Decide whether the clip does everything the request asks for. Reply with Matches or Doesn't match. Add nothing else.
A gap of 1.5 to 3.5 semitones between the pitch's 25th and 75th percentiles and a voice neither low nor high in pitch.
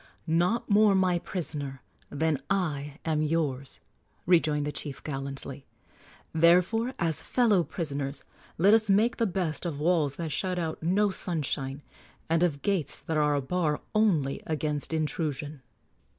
Doesn't match